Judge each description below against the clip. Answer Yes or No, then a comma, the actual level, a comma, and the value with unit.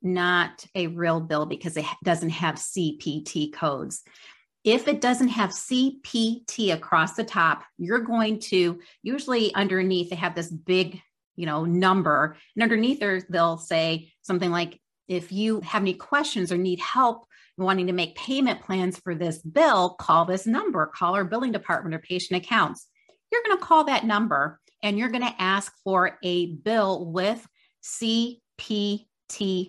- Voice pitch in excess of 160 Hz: Yes, medium, 185 Hz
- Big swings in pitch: No, average, 4.5 semitones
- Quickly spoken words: No, average, 160 wpm